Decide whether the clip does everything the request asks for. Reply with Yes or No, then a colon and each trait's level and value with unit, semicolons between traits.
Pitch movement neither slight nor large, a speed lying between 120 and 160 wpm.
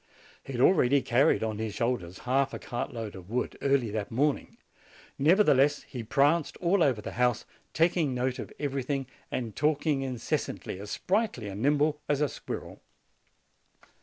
Yes: average, 4.1 semitones; average, 155 wpm